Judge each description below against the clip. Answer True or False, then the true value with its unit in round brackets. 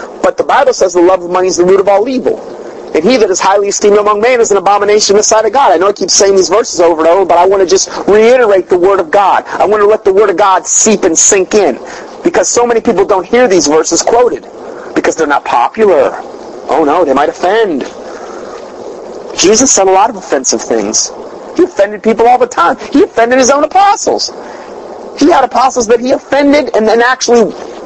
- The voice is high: True (240 Hz)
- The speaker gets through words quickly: True (230 wpm)